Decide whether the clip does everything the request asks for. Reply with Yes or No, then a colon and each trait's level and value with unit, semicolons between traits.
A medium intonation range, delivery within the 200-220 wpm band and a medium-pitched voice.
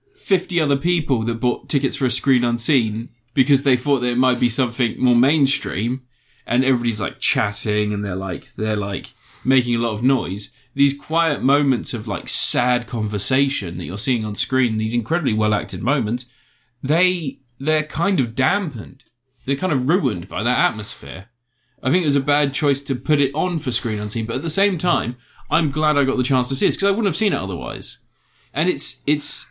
No: average, 3.6 semitones; fast, 205 wpm; low, 130 Hz